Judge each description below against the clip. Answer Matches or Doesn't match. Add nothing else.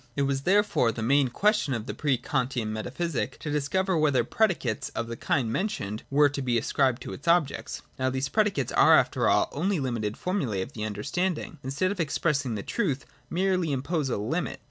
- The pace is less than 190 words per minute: Doesn't match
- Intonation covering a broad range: Matches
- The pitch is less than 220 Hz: Matches